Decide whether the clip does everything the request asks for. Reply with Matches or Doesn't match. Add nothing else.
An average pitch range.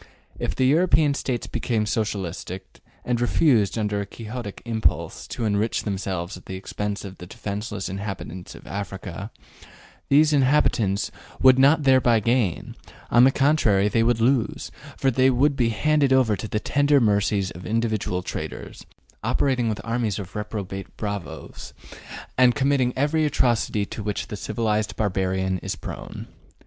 Matches